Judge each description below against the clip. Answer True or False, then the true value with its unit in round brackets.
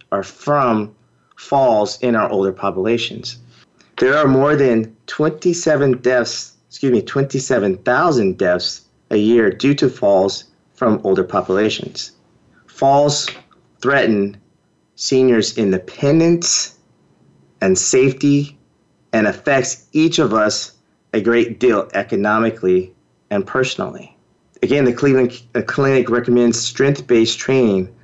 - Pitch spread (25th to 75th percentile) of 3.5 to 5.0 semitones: True (4.1 semitones)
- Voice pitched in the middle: False (120 Hz)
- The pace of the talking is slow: True (105 wpm)